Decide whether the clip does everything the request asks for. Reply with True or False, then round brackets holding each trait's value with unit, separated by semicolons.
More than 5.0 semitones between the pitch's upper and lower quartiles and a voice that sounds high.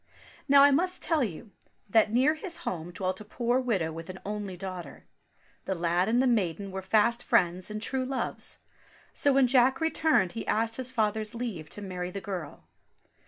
True (5.6 semitones; 215 Hz)